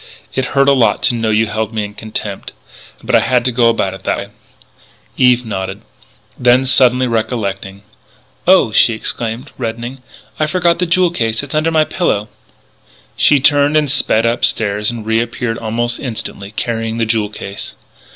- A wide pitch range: No, average, 3.2 semitones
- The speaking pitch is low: Yes, low, 115 Hz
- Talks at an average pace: Yes, average, 170 wpm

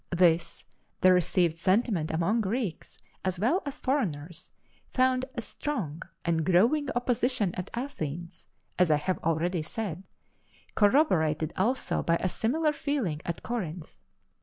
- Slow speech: Yes, slow, 130 wpm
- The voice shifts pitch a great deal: Yes, wide, 6.6 semitones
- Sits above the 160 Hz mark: Yes, medium, 185 Hz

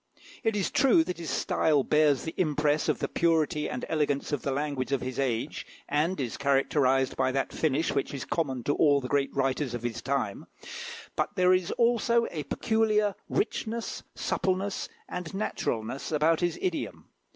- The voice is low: No, medium, 150 Hz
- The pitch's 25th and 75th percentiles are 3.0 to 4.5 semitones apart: No, average, 5.2 semitones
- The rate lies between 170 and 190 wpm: Yes, average, 175 wpm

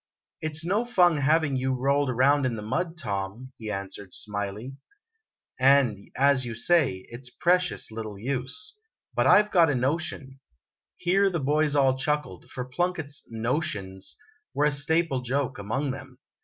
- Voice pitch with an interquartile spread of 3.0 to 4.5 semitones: No, average, 4.9 semitones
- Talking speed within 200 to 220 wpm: No, average, 165 wpm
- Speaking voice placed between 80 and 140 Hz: Yes, low, 135 Hz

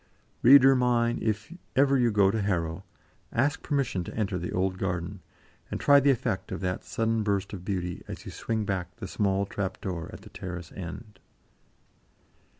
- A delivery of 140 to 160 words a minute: No, average, 175 wpm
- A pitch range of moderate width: Yes, average, 4.1 semitones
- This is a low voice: Yes, low, 100 Hz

